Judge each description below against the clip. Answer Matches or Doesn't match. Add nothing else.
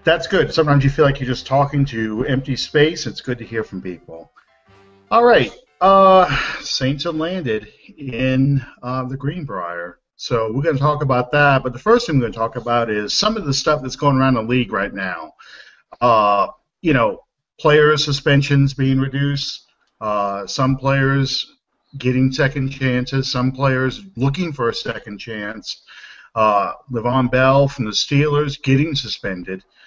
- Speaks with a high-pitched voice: Doesn't match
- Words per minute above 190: Doesn't match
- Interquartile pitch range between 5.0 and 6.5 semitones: Doesn't match